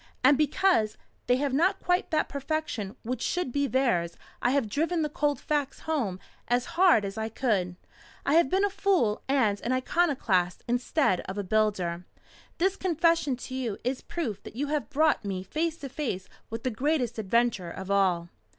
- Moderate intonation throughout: No, wide, 6.7 semitones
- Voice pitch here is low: No, very high, 255 Hz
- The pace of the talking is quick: No, average, 180 wpm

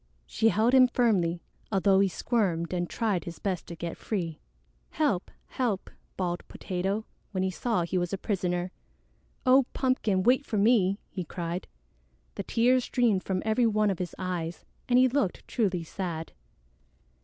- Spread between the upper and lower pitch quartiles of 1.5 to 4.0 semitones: No, average, 4.6 semitones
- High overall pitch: Yes, high, 195 Hz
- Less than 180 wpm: Yes, average, 160 wpm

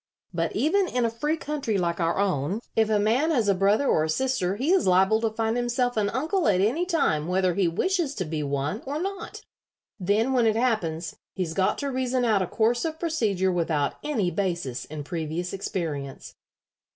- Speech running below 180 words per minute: No, average, 200 wpm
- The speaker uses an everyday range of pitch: No, wide, 6.6 semitones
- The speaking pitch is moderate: No, high, 210 Hz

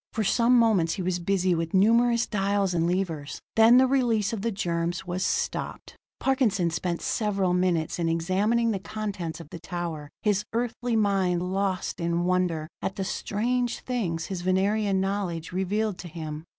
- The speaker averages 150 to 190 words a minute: Yes, average, 165 wpm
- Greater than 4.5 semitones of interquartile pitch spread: No, average, 3.8 semitones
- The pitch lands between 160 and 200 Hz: Yes, high, 190 Hz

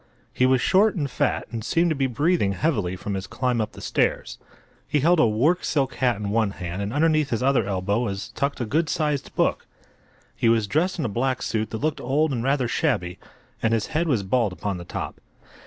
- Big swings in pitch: Yes, wide, 6.1 semitones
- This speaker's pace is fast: Yes, fast, 220 wpm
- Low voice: Yes, low, 125 Hz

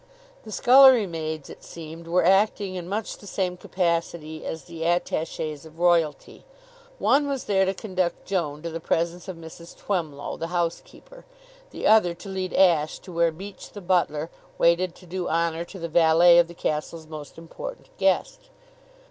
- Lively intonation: No, narrow, 2.6 semitones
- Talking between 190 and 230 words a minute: No, average, 170 wpm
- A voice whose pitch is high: No, medium, 170 Hz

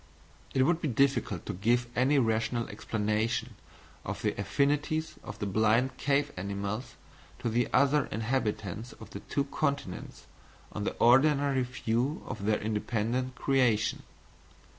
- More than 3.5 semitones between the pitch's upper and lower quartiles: Yes, average, 4.3 semitones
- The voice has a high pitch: No, low, 120 Hz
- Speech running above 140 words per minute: No, slow, 135 wpm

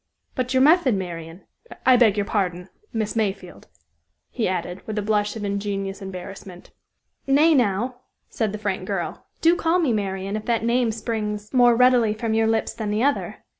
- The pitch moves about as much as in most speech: Yes, average, 3.7 semitones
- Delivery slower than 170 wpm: No, average, 175 wpm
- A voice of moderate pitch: No, high, 215 Hz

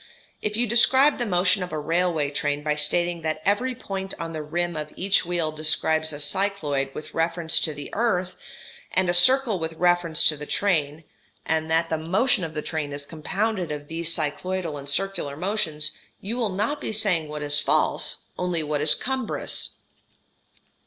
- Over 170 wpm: Yes, average, 180 wpm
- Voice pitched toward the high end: No, medium, 170 Hz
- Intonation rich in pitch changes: No, average, 4.2 semitones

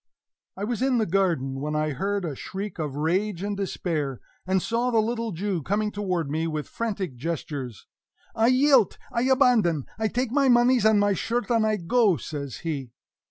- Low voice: No, high, 200 Hz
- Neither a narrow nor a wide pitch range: No, wide, 6.5 semitones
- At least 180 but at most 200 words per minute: Yes, average, 185 wpm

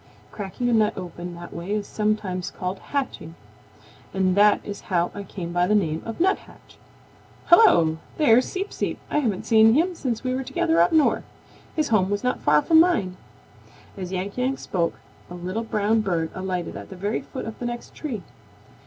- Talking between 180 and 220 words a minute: Yes, average, 190 wpm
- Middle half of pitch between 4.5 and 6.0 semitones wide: Yes, average, 5.1 semitones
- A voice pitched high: Yes, high, 205 Hz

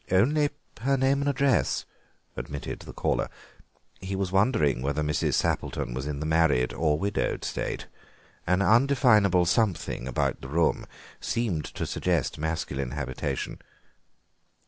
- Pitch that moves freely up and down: Yes, wide, 7.5 semitones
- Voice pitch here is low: Yes, very low, 90 Hz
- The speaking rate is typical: No, slow, 130 wpm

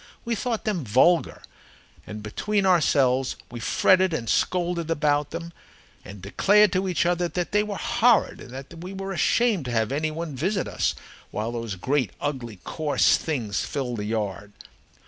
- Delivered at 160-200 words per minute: Yes, average, 165 wpm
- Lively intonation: Yes, wide, 7.5 semitones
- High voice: No, medium, 155 Hz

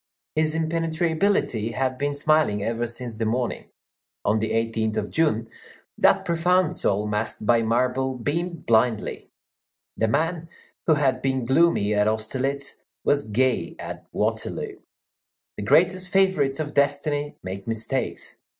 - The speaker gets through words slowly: Yes, slow, 130 wpm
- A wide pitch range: Yes, wide, 5.9 semitones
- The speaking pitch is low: Yes, low, 130 Hz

